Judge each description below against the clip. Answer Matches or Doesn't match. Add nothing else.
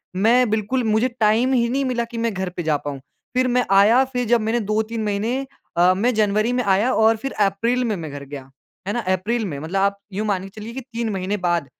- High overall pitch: Matches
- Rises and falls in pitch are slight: Doesn't match